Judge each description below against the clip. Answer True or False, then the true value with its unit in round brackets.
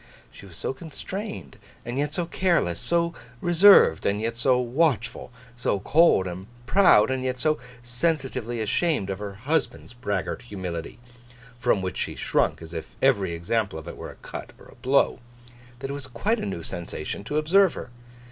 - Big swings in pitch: True (7.1 semitones)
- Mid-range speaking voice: False (120 Hz)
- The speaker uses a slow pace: False (175 wpm)